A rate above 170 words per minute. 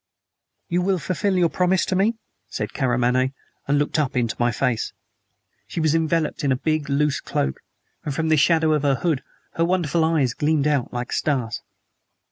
Yes: average, 180 wpm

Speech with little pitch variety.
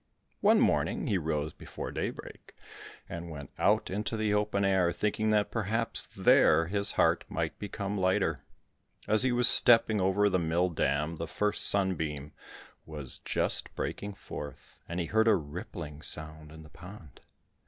No: average, 4.8 semitones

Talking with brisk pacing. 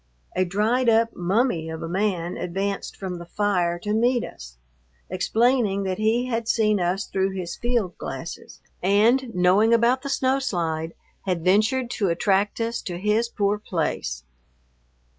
No: average, 155 wpm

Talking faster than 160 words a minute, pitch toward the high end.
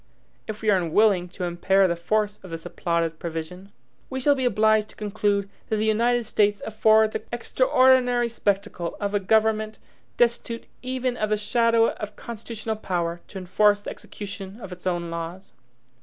Yes: average, 170 wpm; high, 210 Hz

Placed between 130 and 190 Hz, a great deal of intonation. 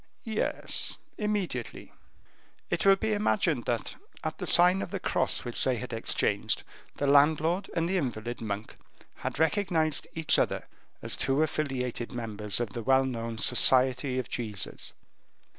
Yes: low, 135 Hz; wide, 5.9 semitones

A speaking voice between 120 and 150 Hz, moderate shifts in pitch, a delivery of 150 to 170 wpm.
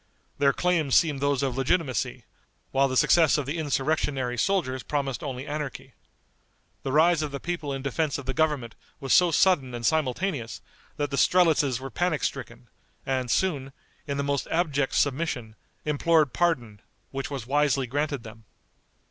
Yes: medium, 140 Hz; average, 3.1 semitones; average, 160 wpm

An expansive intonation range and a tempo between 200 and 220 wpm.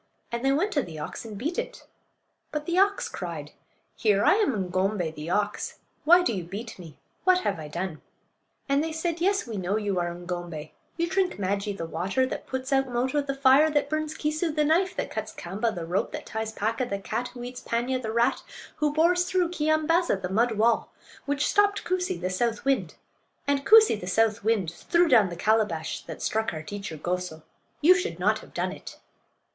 Yes: wide, 8.3 semitones; fast, 205 wpm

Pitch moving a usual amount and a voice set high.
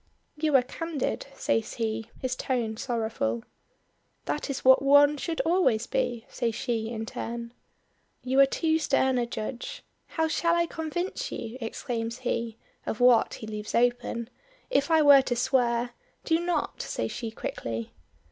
Yes: average, 4.4 semitones; very high, 250 Hz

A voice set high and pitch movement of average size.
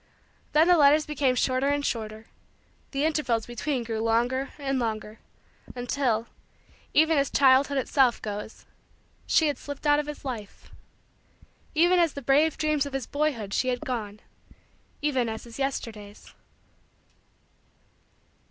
Yes: very high, 270 Hz; average, 4.1 semitones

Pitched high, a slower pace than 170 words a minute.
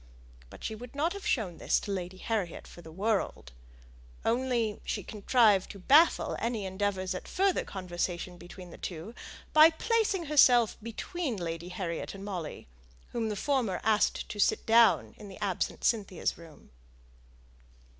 Yes: high, 205 Hz; average, 155 wpm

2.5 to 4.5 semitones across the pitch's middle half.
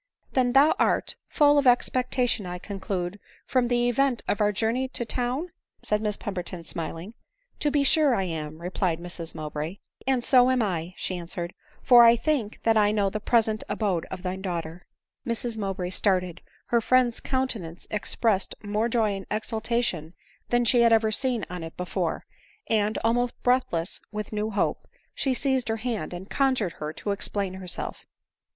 No: average, 5.0 semitones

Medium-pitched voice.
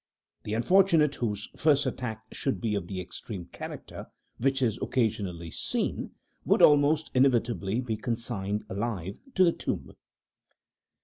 No: low, 115 Hz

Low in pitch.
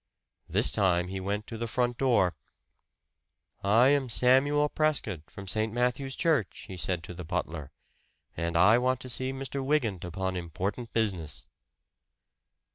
Yes: low, 110 Hz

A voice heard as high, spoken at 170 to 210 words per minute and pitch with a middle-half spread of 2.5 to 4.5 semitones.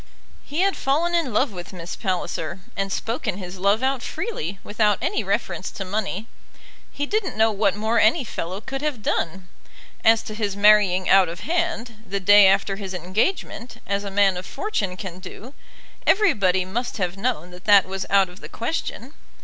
Yes: high, 205 Hz; average, 180 wpm; average, 4.1 semitones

